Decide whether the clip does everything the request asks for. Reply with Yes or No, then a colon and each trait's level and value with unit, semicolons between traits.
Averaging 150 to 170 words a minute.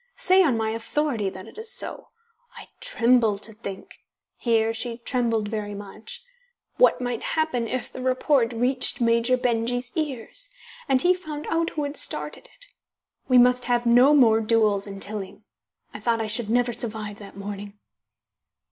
Yes: average, 165 wpm